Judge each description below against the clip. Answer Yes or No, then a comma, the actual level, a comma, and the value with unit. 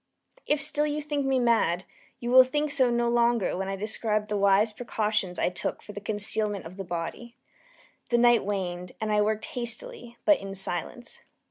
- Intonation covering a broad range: No, average, 3.6 semitones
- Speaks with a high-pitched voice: Yes, high, 220 Hz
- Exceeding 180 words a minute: Yes, average, 190 wpm